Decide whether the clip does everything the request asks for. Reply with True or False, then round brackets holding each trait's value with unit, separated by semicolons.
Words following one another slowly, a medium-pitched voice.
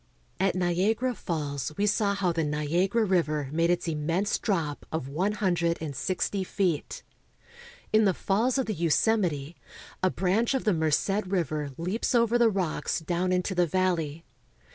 False (160 wpm; 180 Hz)